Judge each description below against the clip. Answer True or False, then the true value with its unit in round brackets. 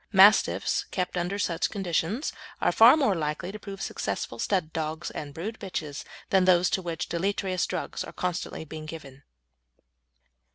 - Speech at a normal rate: True (155 wpm)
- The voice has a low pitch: False (180 Hz)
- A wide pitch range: False (3.7 semitones)